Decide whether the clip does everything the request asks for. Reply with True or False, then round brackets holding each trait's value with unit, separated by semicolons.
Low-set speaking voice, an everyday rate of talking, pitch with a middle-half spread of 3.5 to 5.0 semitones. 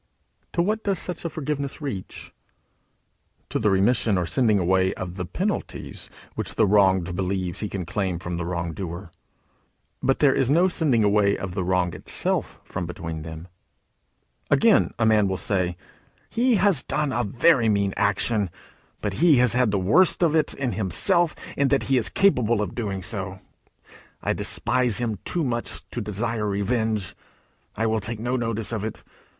False (110 Hz; 170 wpm; 5.5 semitones)